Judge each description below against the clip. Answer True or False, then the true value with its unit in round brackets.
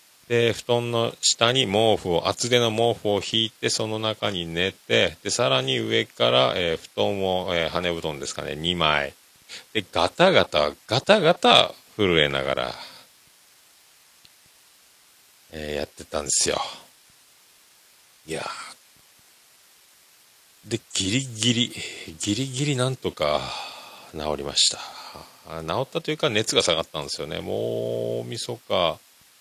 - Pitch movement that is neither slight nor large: False (7.1 semitones)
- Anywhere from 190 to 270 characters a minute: True (235 characters per minute)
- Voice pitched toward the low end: True (100 Hz)